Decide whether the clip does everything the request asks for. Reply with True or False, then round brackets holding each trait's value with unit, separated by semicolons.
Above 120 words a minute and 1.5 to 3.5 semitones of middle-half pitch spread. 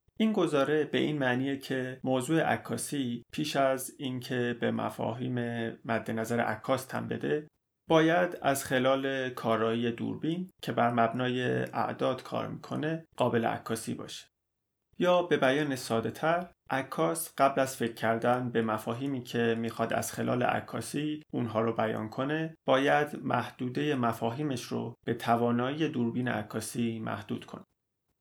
False (130 wpm; 4.1 semitones)